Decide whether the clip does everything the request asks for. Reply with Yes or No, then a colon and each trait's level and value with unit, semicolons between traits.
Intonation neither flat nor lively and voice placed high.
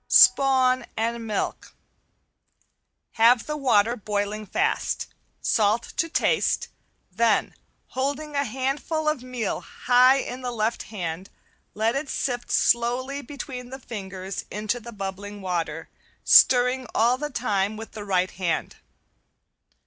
Yes: average, 4.1 semitones; high, 235 Hz